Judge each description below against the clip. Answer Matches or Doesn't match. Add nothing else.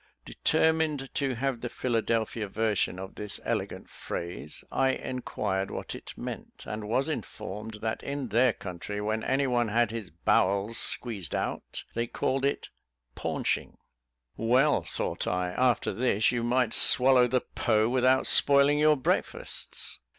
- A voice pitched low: Matches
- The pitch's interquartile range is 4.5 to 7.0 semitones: Doesn't match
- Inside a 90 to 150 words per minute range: Matches